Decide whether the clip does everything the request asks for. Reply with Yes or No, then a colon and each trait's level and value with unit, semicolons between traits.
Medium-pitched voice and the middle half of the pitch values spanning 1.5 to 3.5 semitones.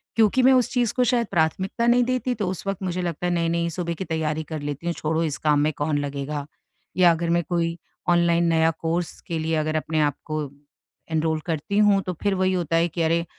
Yes: medium, 170 Hz; average, 2.9 semitones